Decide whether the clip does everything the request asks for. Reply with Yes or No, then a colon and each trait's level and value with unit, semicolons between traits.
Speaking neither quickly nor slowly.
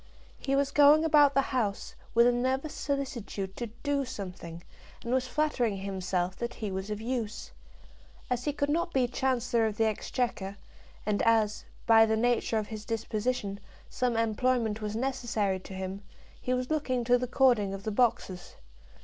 Yes: average, 170 wpm